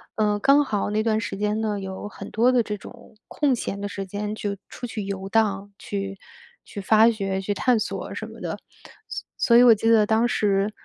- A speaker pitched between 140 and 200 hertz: No, high, 210 Hz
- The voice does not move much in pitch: Yes, narrow, 2.1 semitones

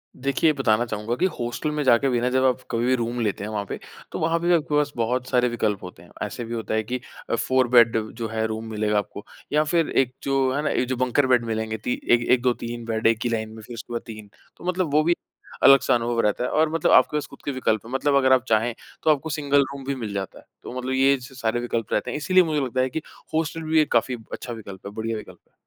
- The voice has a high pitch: No, low, 125 Hz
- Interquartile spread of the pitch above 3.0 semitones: Yes, average, 3.6 semitones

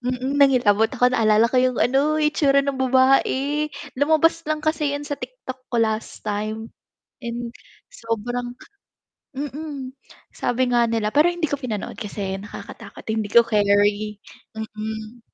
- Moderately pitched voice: No, high, 245 Hz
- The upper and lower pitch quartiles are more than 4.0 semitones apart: Yes, average, 4.5 semitones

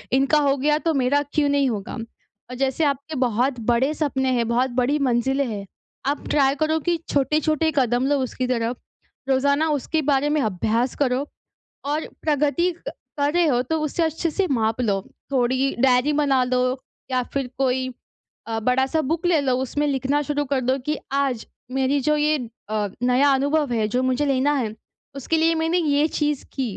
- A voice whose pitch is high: Yes, very high, 275 Hz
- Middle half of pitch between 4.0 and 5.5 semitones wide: No, average, 2.9 semitones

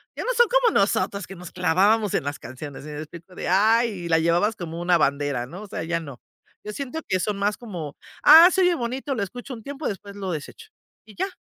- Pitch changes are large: Yes, wide, 5.9 semitones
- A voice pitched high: Yes, high, 195 Hz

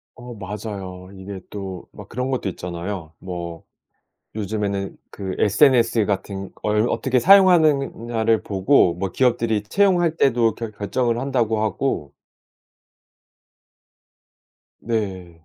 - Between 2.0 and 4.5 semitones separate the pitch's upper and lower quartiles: Yes, average, 4.1 semitones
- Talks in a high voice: No, low, 105 Hz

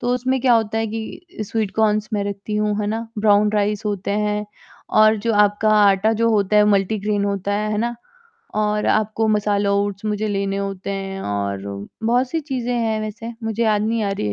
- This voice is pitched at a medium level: No, high, 210 Hz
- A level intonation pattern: Yes, narrow, 1.6 semitones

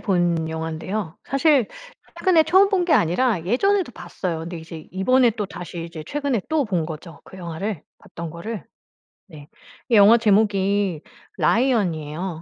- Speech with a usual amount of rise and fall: No, wide, 6.5 semitones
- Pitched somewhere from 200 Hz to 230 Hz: No, high, 190 Hz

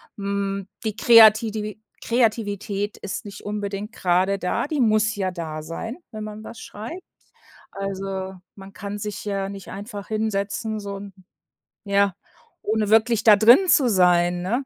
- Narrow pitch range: Yes, narrow, 1.8 semitones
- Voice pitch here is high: Yes, high, 205 Hz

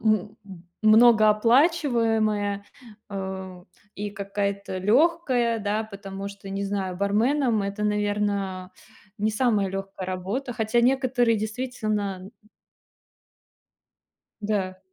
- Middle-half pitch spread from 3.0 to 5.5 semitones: No, narrow, 2.6 semitones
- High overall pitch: Yes, high, 210 Hz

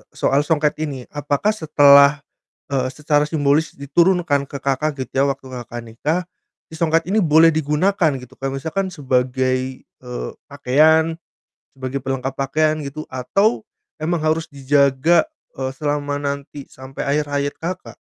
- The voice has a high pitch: No, medium, 145 Hz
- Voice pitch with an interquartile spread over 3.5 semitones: No, average, 2.9 semitones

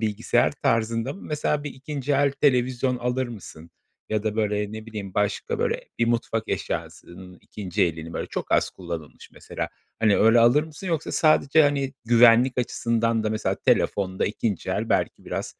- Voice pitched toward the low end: Yes, low, 115 Hz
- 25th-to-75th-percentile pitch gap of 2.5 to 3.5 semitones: No, average, 4.2 semitones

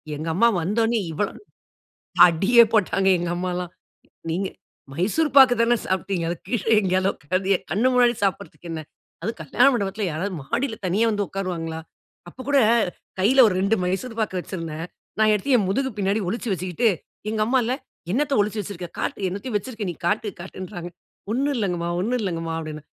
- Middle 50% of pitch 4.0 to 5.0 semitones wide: Yes, average, 4.4 semitones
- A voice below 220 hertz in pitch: Yes, high, 195 Hz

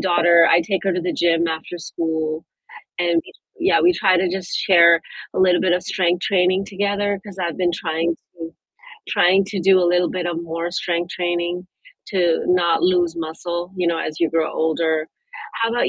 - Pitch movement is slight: Yes, narrow, 1.8 semitones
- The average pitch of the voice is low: No, medium, 175 Hz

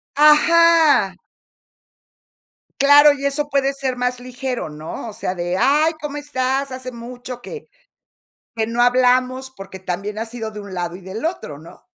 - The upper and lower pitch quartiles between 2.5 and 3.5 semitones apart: No, average, 4.8 semitones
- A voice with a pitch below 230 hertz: No, very high, 255 Hz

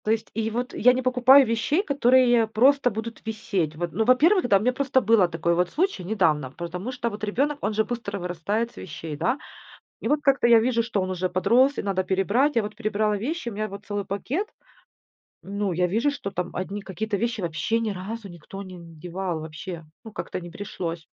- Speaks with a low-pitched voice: No, high, 210 Hz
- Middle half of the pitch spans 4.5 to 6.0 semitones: Yes, average, 4.8 semitones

